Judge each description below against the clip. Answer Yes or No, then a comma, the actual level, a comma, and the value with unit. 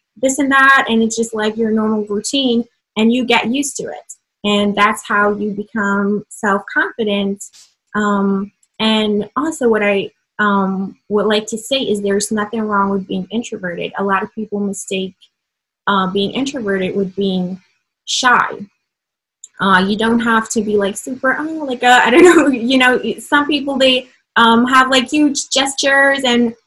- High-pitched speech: Yes, high, 220 Hz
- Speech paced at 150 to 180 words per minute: Yes, average, 170 wpm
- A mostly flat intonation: No, average, 3.8 semitones